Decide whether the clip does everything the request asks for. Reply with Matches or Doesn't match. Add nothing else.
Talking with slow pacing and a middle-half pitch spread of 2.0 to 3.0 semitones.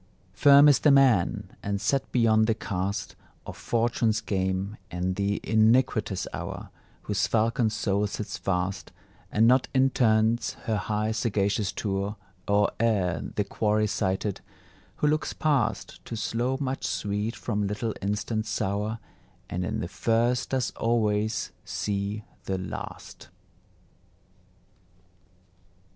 Matches